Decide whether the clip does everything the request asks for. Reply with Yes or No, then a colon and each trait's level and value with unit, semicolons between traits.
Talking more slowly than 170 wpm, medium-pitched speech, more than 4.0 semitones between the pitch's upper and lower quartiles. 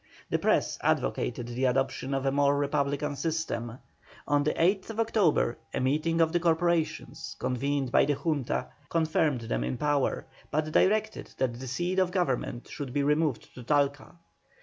No: average, 160 wpm; medium, 145 Hz; average, 3.7 semitones